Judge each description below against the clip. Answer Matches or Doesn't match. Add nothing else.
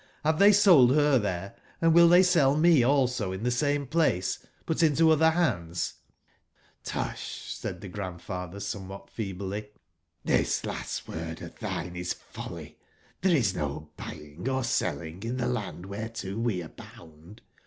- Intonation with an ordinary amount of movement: Doesn't match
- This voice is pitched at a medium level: Doesn't match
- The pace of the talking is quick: Doesn't match